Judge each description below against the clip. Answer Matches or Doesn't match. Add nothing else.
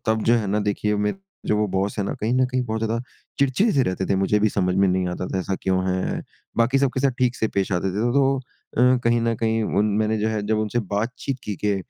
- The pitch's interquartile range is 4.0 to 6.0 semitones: Doesn't match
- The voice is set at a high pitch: Doesn't match